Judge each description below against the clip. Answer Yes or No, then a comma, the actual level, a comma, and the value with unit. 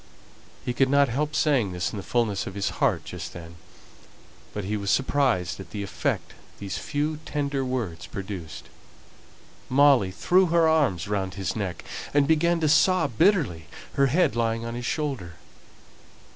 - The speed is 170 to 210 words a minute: No, average, 160 wpm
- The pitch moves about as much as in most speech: No, wide, 7.1 semitones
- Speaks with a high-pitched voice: No, low, 120 Hz